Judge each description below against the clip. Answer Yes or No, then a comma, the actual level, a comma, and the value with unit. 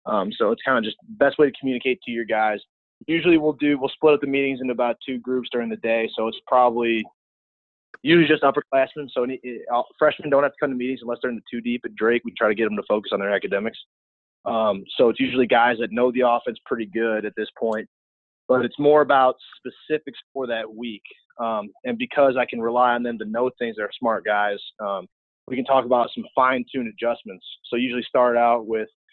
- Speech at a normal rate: No, fast, 230 wpm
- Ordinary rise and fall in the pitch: Yes, average, 3.1 semitones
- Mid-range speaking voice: No, low, 125 Hz